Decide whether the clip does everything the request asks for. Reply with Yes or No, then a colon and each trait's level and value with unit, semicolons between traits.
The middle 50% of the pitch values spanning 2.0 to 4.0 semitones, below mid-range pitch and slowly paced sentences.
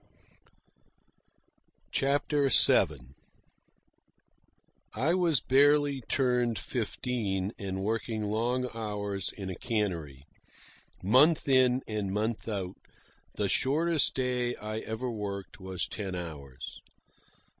No: average, 4.6 semitones; low, 110 Hz; slow, 95 wpm